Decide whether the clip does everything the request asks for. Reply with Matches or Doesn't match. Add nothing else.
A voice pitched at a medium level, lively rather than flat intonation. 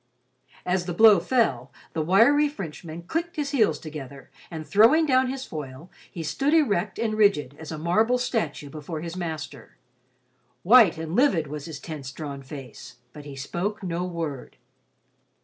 Matches